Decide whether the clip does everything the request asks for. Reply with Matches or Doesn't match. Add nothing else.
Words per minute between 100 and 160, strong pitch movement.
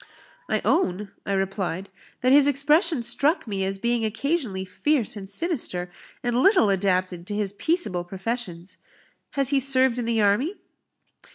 Matches